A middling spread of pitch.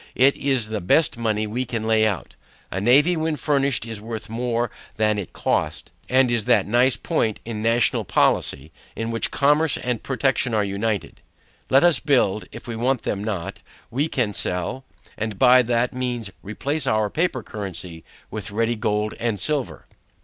Yes: average, 3.6 semitones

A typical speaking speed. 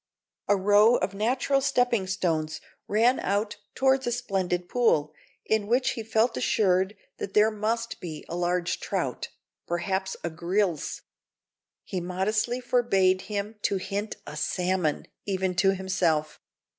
No: slow, 130 wpm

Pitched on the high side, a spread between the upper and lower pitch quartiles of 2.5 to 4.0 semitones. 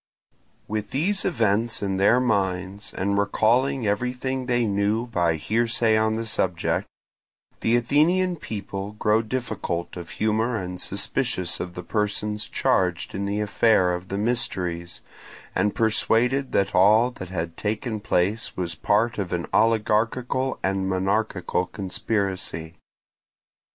No: low, 105 Hz; average, 3.6 semitones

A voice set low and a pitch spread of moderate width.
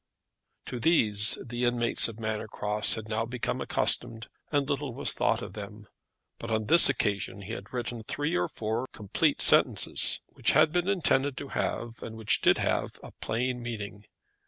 Yes: low, 115 Hz; average, 3.0 semitones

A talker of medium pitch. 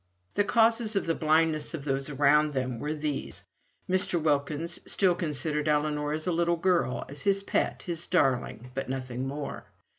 Yes: medium, 150 Hz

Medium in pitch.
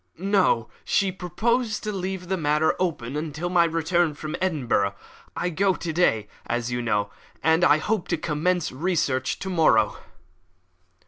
Yes: medium, 165 Hz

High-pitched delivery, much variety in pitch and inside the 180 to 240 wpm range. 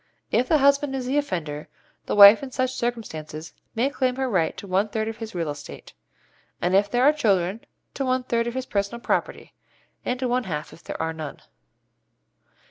Yes: high, 225 Hz; wide, 6.1 semitones; average, 200 wpm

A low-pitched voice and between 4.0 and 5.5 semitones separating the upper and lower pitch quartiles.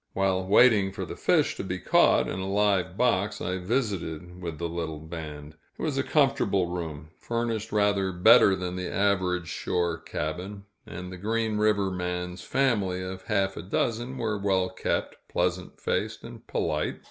No: very low, 95 Hz; narrow, 2.6 semitones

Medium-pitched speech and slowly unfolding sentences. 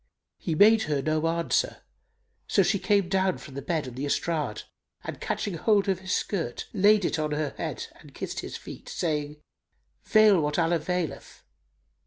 No: medium, 170 Hz; average, 175 wpm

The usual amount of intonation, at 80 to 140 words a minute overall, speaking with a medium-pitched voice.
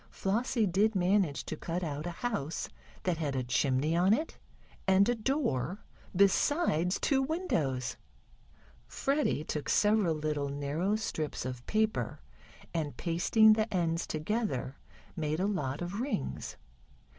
No: wide, 6.3 semitones; slow, 135 wpm; medium, 175 Hz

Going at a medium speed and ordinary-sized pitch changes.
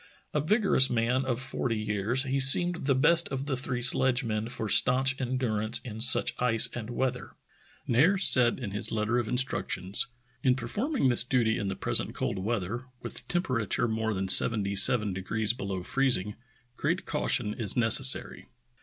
Yes: average, 170 wpm; average, 3.5 semitones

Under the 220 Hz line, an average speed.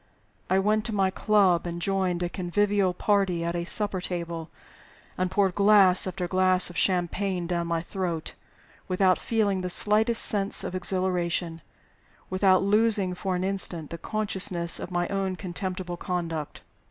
Yes: medium, 185 Hz; average, 155 wpm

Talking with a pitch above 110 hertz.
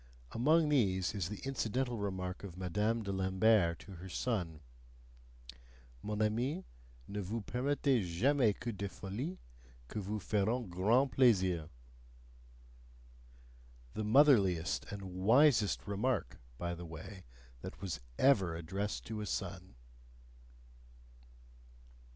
No: low, 105 Hz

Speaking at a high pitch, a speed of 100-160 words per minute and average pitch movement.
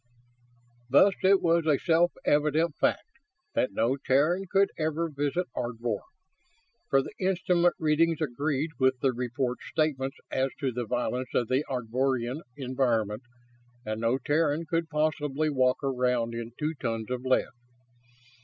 No: low, 135 Hz; average, 140 wpm; average, 4.2 semitones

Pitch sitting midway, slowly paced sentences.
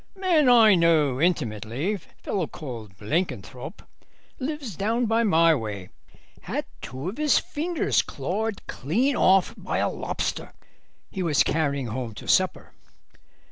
Yes: medium, 170 Hz; slow, 125 wpm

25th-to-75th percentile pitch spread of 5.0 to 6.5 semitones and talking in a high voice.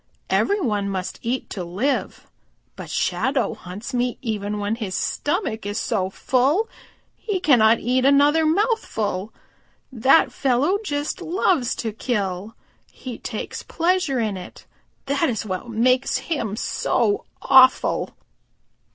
Yes: wide, 5.6 semitones; high, 245 Hz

